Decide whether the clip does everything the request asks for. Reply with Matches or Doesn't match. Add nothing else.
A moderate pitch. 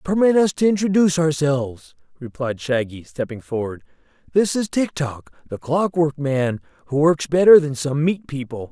Matches